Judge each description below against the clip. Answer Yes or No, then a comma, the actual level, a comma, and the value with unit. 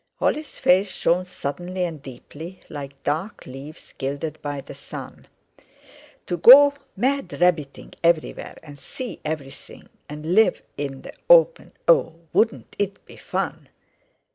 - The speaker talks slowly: Yes, slow, 125 wpm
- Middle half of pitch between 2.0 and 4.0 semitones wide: No, wide, 5.5 semitones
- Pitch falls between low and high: Yes, medium, 165 Hz